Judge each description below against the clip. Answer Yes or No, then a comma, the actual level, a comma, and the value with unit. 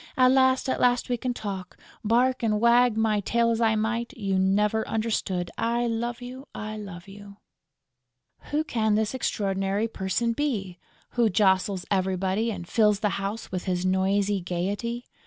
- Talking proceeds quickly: No, average, 160 wpm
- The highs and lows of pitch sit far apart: No, average, 3.4 semitones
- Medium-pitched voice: No, high, 215 Hz